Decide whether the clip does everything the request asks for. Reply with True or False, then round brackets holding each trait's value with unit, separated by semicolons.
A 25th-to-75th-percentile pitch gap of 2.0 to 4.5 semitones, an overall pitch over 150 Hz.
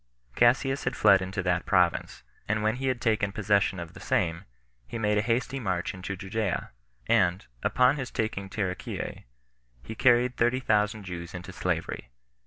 False (4.2 semitones; 105 Hz)